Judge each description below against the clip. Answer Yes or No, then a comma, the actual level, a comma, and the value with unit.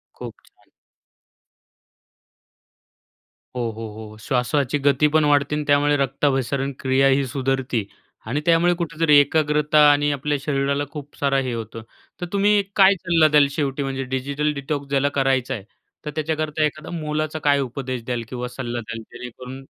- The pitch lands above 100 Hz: Yes, medium, 140 Hz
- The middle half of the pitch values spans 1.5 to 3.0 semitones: Yes, narrow, 2.5 semitones